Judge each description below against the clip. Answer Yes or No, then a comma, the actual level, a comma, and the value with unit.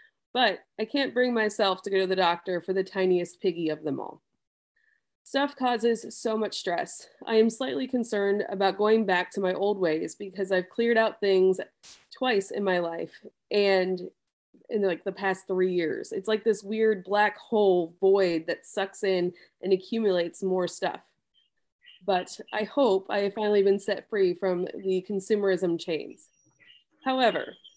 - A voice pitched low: No, high, 195 Hz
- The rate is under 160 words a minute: No, average, 165 wpm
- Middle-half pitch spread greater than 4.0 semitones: No, average, 2.9 semitones